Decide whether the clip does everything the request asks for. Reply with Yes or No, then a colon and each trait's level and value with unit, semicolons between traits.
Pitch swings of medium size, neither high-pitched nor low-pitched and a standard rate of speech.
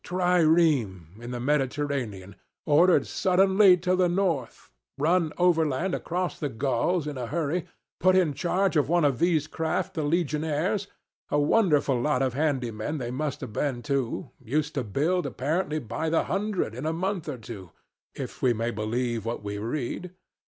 No: wide, 5.9 semitones; medium, 150 Hz; average, 165 wpm